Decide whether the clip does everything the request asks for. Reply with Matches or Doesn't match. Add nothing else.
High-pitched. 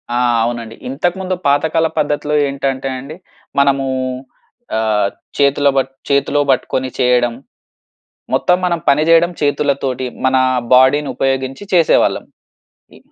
Doesn't match